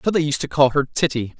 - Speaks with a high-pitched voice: No, medium, 145 Hz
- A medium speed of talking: No, fast, 300 wpm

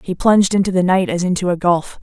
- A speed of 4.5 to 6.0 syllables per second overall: No, 6.3 syllables/s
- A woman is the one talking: Yes, female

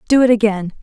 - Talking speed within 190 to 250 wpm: Yes, fast, 220 wpm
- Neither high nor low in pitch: No, high, 220 Hz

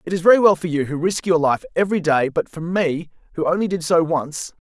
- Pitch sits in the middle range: Yes, medium, 170 Hz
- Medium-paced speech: No, fast, 255 wpm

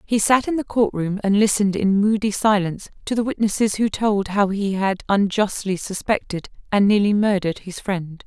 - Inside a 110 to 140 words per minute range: No, average, 190 wpm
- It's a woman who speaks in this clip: Yes, female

